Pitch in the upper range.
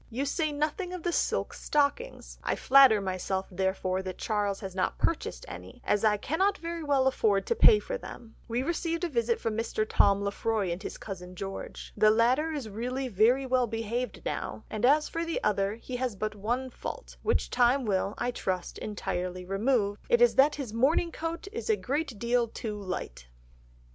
Yes: high, 235 Hz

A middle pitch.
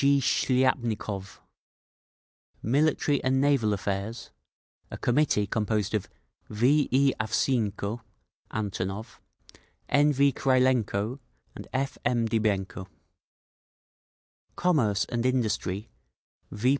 No: low, 115 Hz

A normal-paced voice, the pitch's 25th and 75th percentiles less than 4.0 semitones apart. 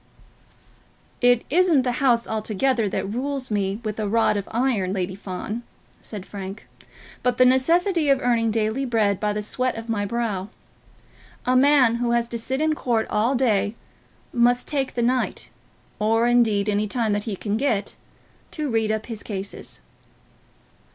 Yes: average, 165 wpm; average, 3.3 semitones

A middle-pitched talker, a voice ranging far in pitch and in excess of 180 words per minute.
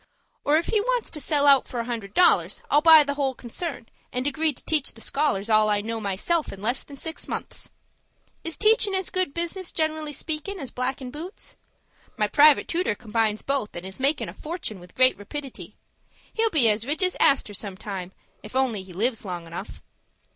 No: very high, 270 Hz; wide, 6.7 semitones; average, 200 wpm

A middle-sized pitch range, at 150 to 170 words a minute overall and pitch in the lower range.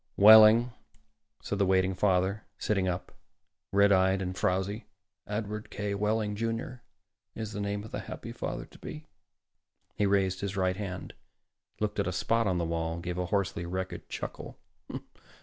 No: narrow, 2.3 semitones; average, 160 wpm; low, 100 Hz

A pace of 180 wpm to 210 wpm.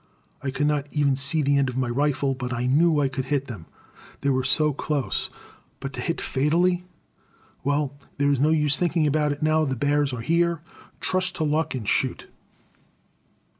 Yes: average, 190 wpm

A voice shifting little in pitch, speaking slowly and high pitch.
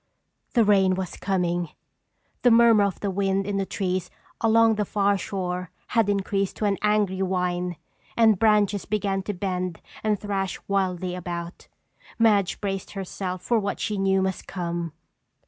No: narrow, 2.2 semitones; average, 155 wpm; high, 195 Hz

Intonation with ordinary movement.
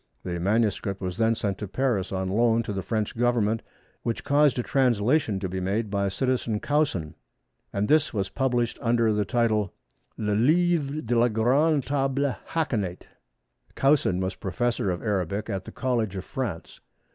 Yes: average, 4.6 semitones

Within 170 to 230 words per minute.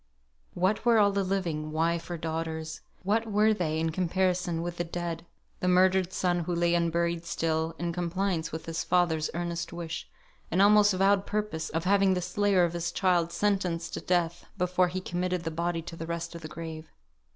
Yes: average, 190 wpm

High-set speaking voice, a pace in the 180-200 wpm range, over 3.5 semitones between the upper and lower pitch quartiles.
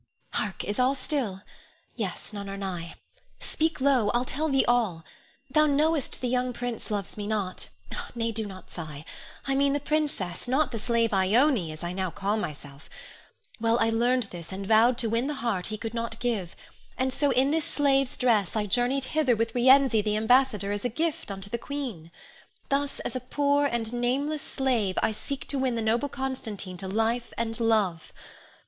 Yes: high, 235 Hz; average, 190 wpm; average, 4.6 semitones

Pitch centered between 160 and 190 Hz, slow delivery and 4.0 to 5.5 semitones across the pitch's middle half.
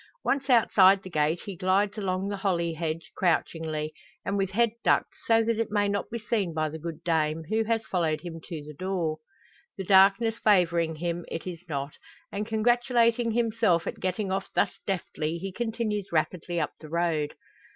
No: medium, 185 Hz; average, 185 wpm; average, 4.6 semitones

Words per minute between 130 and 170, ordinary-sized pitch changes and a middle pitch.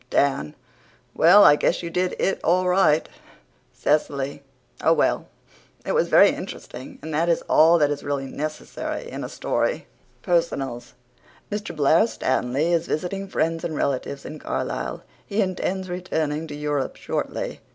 Yes: average, 150 wpm; average, 3.9 semitones; medium, 160 Hz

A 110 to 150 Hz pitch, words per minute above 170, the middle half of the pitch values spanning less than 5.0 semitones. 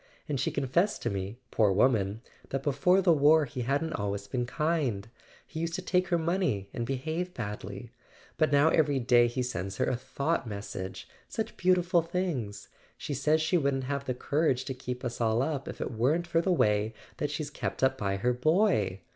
No: low, 135 Hz; average, 195 wpm; wide, 5.5 semitones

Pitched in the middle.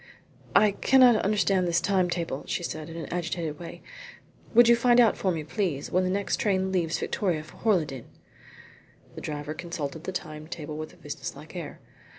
Yes: medium, 175 Hz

